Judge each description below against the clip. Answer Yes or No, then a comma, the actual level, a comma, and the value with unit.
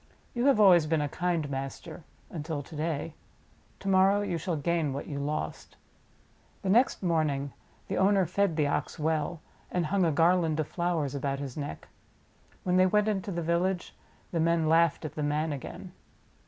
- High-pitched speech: No, medium, 165 Hz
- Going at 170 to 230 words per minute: Yes, average, 180 wpm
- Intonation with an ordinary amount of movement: Yes, average, 3.5 semitones